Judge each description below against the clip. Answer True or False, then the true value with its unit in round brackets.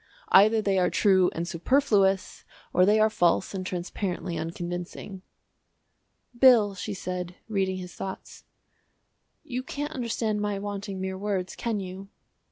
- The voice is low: False (195 Hz)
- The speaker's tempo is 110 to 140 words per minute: True (135 wpm)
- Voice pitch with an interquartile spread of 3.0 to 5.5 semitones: False (2.5 semitones)